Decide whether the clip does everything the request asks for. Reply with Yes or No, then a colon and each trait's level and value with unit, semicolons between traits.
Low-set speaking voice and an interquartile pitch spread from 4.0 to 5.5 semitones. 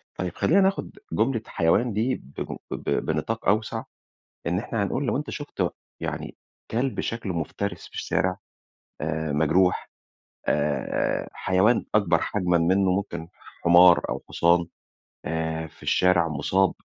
Yes: very low, 90 Hz; average, 4.8 semitones